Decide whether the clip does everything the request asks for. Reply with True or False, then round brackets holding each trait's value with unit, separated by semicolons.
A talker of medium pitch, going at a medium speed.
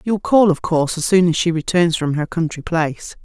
False (170 Hz; 240 wpm)